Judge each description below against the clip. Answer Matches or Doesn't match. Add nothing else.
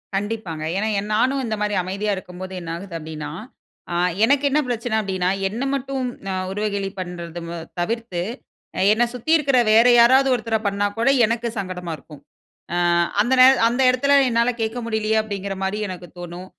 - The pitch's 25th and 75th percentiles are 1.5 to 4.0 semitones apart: Doesn't match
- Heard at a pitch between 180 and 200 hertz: Doesn't match